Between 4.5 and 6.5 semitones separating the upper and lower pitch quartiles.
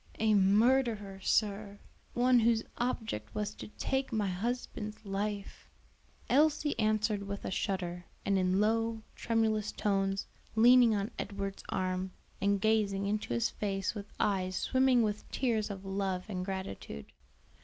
No: narrow, 2.4 semitones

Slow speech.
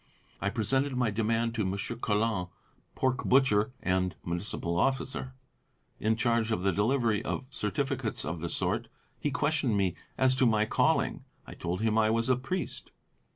No: average, 160 wpm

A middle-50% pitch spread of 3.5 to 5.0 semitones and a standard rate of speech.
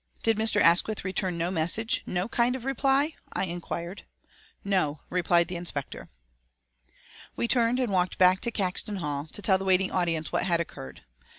Yes: average, 4.5 semitones; average, 170 wpm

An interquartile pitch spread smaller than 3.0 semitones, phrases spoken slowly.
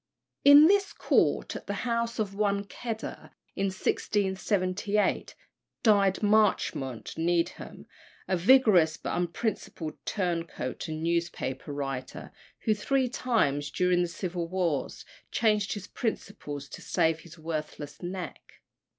No: average, 4.4 semitones; slow, 115 wpm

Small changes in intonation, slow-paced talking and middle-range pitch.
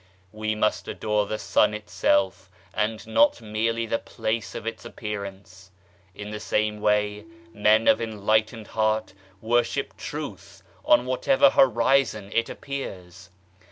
No: narrow, 1.7 semitones; slow, 125 wpm; low, 110 Hz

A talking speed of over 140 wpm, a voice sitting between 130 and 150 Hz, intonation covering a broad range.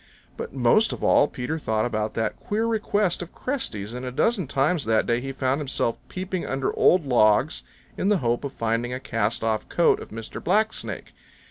Yes: average, 200 wpm; low, 135 Hz; wide, 7.8 semitones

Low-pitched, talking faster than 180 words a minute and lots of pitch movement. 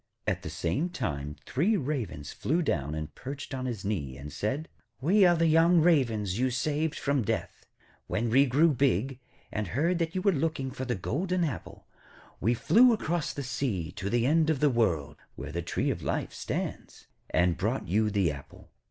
Yes: low, 130 Hz; average, 190 wpm; wide, 8.1 semitones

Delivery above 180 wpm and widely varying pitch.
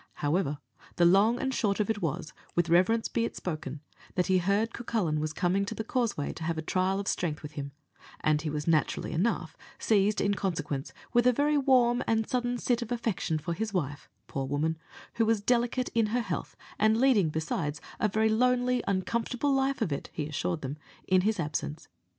Yes: average, 200 wpm; wide, 6.6 semitones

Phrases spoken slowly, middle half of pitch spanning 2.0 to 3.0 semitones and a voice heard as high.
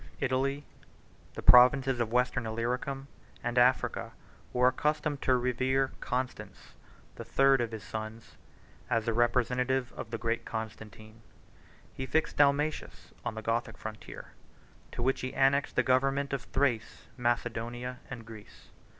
No: slow, 130 wpm; average, 2.7 semitones; low, 125 Hz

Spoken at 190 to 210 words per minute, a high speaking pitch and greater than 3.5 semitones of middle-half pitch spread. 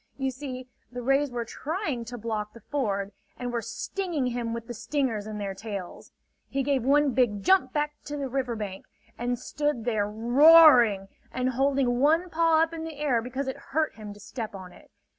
Yes: average, 200 wpm; very high, 250 Hz; average, 4.4 semitones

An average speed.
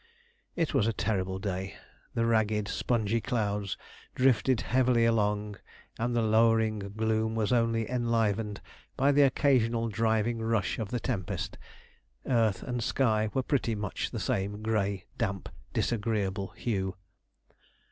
No: slow, 130 wpm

